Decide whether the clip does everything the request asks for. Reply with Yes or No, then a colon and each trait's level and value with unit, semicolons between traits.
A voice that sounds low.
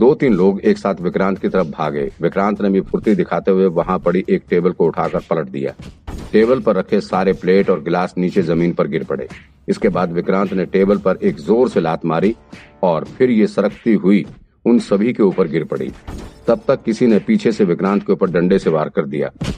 Yes: very low, 95 Hz